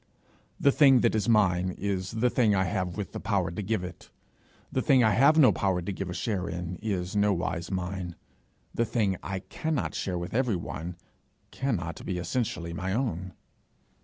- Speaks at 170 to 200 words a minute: Yes, average, 180 wpm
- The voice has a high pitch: No, very low, 95 Hz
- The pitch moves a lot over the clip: No, average, 4.0 semitones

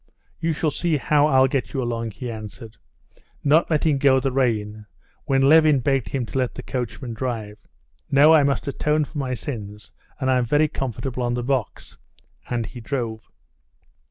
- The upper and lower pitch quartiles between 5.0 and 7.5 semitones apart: No, average, 3.5 semitones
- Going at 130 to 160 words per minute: No, average, 175 wpm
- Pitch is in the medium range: No, low, 130 Hz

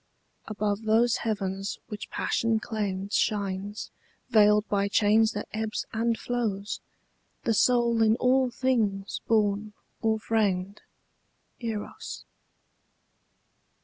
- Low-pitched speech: No, high, 215 Hz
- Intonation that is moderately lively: No, narrow, 1.9 semitones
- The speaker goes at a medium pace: No, slow, 100 wpm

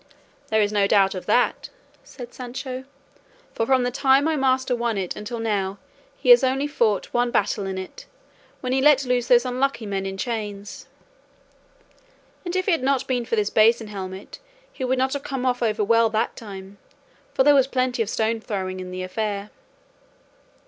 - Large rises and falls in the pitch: No, average, 4.2 semitones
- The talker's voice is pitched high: Yes, high, 235 Hz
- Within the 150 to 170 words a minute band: No, average, 185 wpm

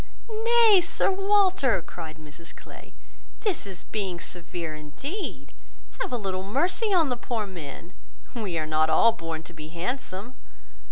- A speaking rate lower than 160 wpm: Yes, average, 150 wpm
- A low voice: No, high, 195 Hz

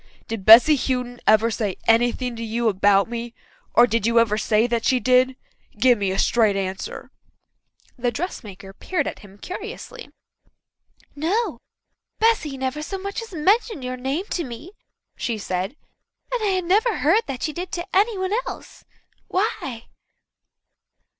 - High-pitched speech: Yes, very high, 250 Hz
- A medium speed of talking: Yes, average, 150 wpm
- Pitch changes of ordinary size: No, wide, 8.1 semitones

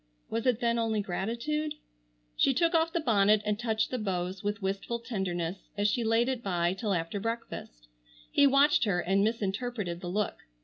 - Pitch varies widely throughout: No, average, 3.8 semitones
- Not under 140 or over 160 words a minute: No, average, 180 wpm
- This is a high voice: Yes, high, 215 Hz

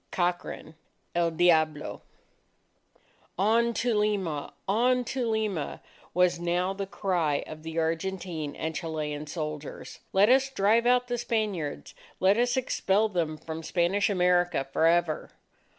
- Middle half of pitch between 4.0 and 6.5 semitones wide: Yes, average, 5.0 semitones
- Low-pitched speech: No, medium, 180 Hz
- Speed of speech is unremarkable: No, slow, 130 wpm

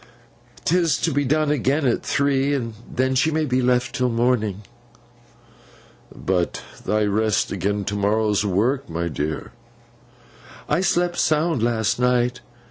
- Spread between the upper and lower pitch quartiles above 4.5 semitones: Yes, wide, 5.4 semitones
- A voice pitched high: No, low, 125 Hz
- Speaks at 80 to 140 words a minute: Yes, slow, 135 wpm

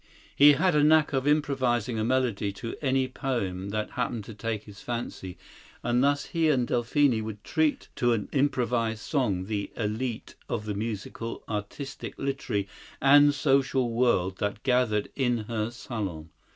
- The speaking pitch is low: Yes, low, 120 Hz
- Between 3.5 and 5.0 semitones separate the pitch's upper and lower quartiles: Yes, average, 4.2 semitones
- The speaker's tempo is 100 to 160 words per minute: Yes, average, 155 wpm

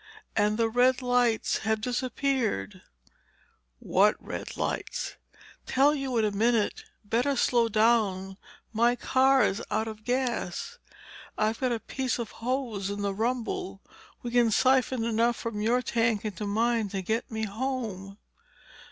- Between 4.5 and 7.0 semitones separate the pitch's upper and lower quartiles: No, average, 2.8 semitones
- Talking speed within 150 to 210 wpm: No, average, 140 wpm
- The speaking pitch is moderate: No, high, 230 Hz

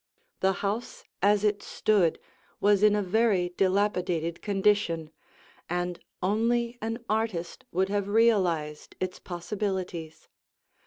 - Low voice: No, high, 195 Hz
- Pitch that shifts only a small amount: No, average, 3.1 semitones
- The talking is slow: Yes, slow, 110 wpm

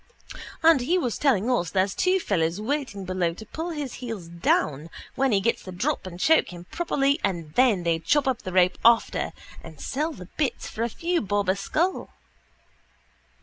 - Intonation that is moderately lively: No, wide, 7.6 semitones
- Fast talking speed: No, average, 190 wpm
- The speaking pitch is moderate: No, high, 220 Hz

